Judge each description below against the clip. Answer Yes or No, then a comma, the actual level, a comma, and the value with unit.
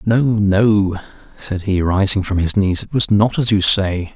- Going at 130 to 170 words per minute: No, average, 200 wpm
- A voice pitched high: No, low, 100 Hz